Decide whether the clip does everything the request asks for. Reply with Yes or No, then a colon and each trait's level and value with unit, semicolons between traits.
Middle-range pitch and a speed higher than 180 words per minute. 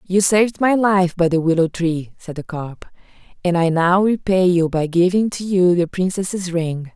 Yes: medium, 180 Hz; average, 200 wpm